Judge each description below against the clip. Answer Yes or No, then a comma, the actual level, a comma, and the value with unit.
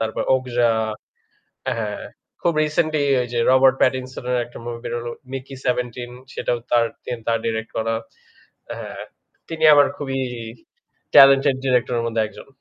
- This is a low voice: Yes, low, 125 Hz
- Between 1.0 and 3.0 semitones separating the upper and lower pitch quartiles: Yes, narrow, 2.4 semitones